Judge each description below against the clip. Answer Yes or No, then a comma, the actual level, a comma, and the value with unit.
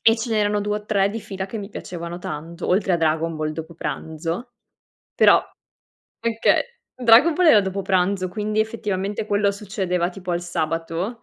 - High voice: Yes, high, 195 Hz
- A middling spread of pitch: Yes, average, 3.7 semitones